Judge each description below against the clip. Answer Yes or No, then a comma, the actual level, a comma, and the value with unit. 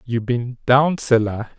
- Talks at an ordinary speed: Yes, average, 150 wpm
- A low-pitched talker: Yes, low, 125 Hz